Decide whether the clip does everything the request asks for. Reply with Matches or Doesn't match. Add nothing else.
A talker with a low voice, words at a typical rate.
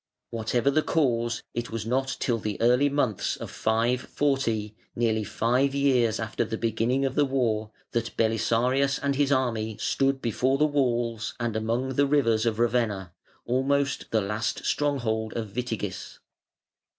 Matches